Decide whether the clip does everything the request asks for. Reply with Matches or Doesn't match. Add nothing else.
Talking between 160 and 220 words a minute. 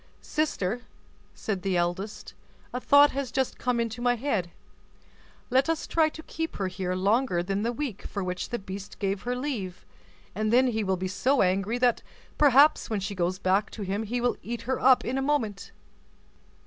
Matches